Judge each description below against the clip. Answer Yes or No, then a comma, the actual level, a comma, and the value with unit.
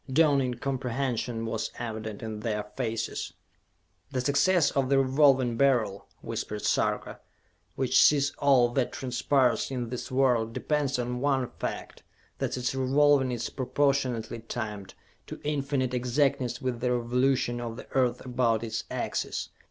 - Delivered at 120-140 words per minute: Yes, slow, 135 wpm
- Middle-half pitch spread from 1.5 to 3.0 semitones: Yes, narrow, 2.6 semitones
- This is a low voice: Yes, low, 125 Hz